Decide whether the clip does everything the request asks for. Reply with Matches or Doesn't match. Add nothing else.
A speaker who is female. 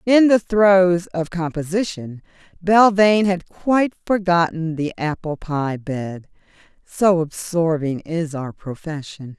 Matches